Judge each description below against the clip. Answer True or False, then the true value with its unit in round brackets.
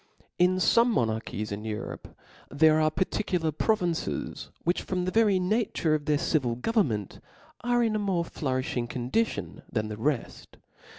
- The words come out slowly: False (160 wpm)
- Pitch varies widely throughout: True (7.8 semitones)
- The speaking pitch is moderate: True (160 Hz)